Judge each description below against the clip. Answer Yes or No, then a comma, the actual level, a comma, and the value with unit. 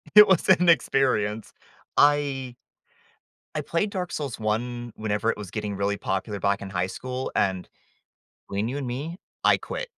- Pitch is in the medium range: No, low, 120 Hz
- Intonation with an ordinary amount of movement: No, wide, 6.0 semitones